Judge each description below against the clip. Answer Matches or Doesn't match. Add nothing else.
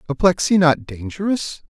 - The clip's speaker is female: Doesn't match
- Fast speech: Doesn't match